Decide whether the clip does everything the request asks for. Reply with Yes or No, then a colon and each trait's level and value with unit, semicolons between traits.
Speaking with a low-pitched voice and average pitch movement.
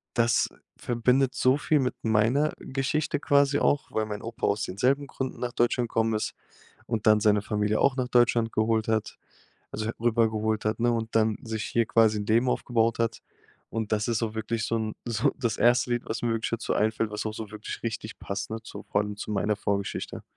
No: low, 115 Hz; narrow, 2.0 semitones